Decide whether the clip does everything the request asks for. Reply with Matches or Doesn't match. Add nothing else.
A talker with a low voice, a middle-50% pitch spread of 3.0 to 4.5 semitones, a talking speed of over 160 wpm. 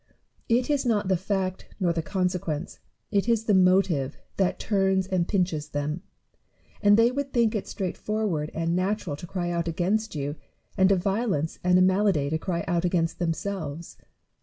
Doesn't match